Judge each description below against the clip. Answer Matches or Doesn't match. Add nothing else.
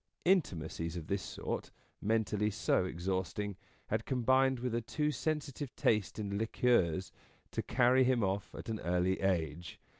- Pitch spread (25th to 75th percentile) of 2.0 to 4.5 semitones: Doesn't match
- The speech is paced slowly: Doesn't match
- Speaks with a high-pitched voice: Doesn't match